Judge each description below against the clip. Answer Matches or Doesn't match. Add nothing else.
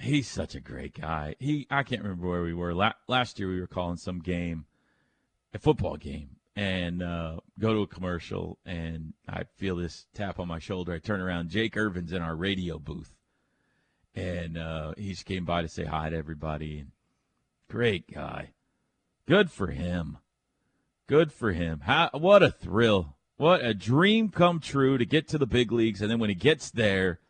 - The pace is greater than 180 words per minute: Matches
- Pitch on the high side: Doesn't match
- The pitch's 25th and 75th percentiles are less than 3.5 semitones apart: Doesn't match